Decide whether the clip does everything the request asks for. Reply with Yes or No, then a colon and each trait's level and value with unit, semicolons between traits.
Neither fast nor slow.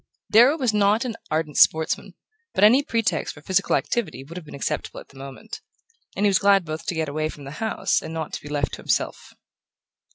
No: fast, 220 wpm